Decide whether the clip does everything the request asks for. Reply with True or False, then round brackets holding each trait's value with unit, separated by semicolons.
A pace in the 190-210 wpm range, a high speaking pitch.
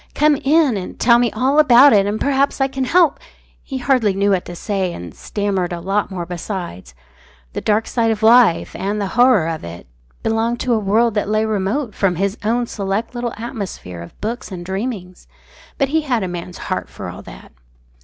True (205 wpm; 215 Hz)